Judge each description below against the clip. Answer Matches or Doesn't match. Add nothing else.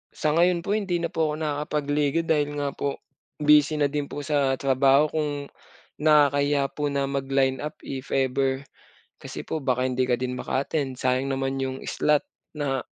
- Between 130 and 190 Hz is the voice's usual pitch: Matches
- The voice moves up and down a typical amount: Doesn't match